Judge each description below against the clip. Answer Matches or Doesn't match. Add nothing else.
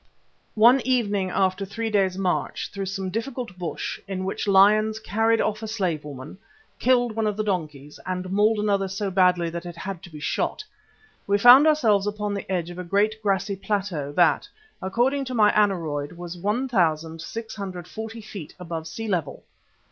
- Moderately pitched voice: Doesn't match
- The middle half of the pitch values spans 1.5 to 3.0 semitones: Doesn't match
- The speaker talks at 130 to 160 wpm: Doesn't match